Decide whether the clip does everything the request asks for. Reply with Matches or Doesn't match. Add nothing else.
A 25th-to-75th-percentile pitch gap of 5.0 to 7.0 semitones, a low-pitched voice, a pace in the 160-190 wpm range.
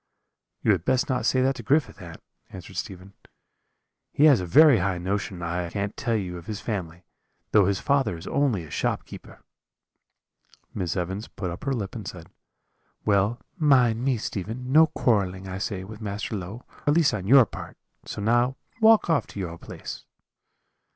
Matches